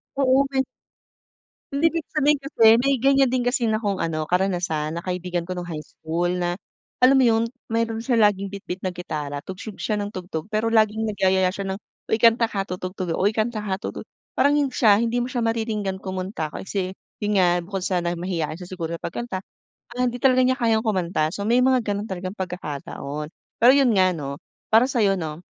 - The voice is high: Yes, high, 200 Hz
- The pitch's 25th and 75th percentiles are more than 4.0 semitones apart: Yes, average, 4.7 semitones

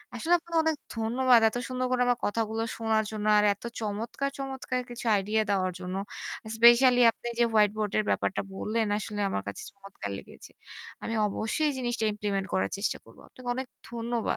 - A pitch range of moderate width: Yes, average, 3.0 semitones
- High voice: Yes, high, 225 Hz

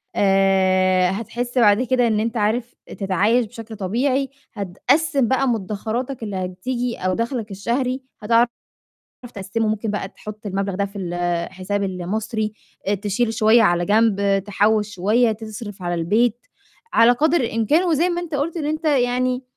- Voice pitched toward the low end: No, high, 220 Hz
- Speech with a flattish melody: No, average, 3.8 semitones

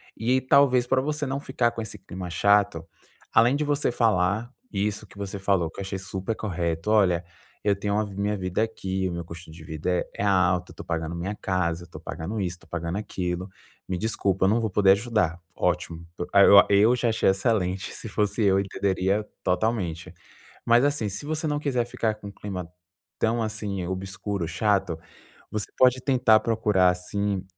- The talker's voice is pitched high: No, low, 100 Hz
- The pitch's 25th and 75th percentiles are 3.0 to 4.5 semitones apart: Yes, average, 3.7 semitones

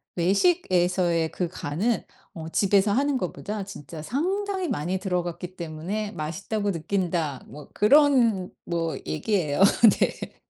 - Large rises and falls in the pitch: No, average, 4.5 semitones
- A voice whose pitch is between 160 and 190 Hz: Yes, medium, 185 Hz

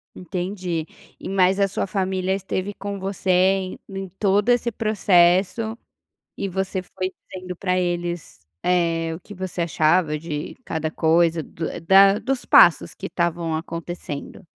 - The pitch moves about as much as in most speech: No, narrow, 2.3 semitones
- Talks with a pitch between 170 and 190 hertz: Yes, medium, 185 Hz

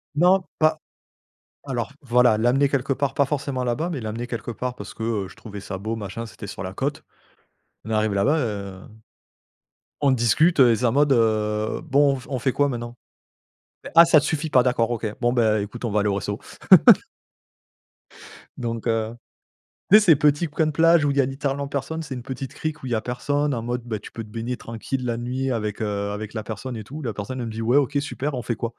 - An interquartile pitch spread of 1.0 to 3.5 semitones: No, average, 4.1 semitones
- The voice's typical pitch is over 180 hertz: No, low, 125 Hz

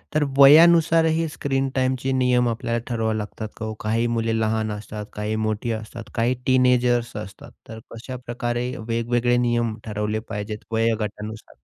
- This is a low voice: Yes, low, 115 Hz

